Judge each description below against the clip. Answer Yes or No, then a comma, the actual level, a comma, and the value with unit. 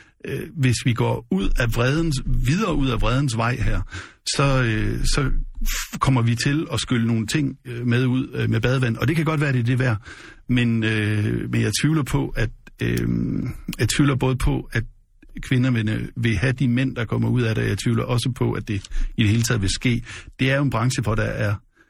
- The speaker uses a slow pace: No, average, 205 wpm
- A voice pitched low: Yes, low, 120 Hz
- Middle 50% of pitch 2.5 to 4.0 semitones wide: Yes, average, 2.9 semitones